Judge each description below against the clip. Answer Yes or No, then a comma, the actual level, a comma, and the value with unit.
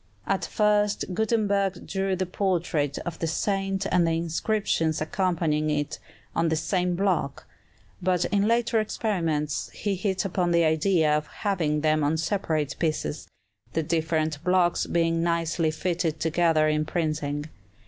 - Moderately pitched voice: Yes, medium, 170 Hz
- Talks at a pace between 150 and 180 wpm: No, average, 140 wpm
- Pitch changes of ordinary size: Yes, average, 3.6 semitones